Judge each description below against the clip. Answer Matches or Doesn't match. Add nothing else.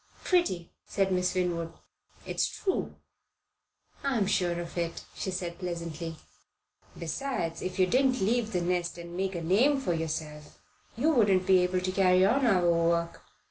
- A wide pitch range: Doesn't match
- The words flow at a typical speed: Matches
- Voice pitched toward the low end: Doesn't match